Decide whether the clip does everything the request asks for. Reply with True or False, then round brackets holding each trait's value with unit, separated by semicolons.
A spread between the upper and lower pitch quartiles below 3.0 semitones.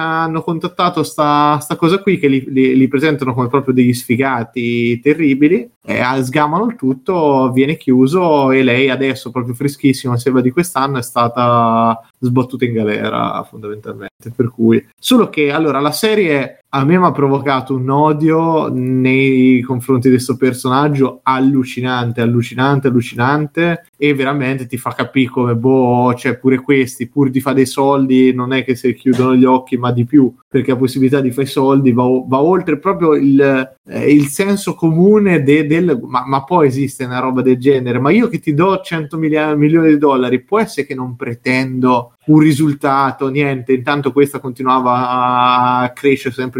True (2.6 semitones)